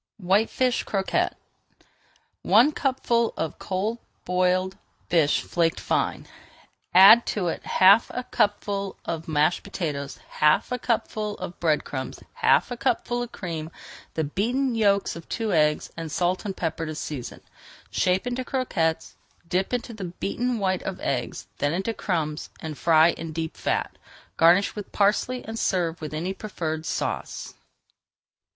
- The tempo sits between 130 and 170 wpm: Yes, average, 150 wpm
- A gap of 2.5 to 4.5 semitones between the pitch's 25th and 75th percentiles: No, average, 5.2 semitones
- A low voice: No, medium, 185 Hz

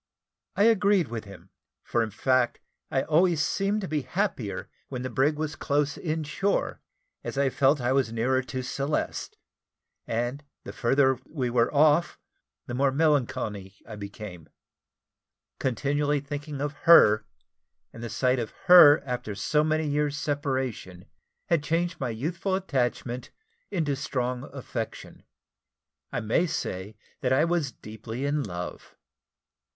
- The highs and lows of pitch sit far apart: No, average, 4.2 semitones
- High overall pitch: No, low, 135 Hz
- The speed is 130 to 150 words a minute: Yes, average, 145 wpm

